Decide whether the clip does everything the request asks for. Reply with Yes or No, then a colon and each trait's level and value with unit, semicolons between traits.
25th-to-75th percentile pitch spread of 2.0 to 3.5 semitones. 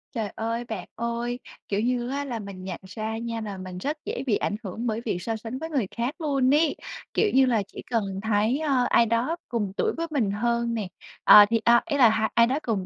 Yes: average, 2.9 semitones